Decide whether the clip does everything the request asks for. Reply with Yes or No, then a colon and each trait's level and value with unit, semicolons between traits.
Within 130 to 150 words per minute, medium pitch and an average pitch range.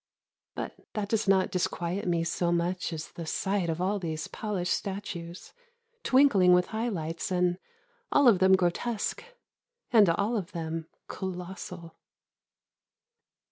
Yes: slow, 135 wpm; medium, 180 Hz; average, 3.0 semitones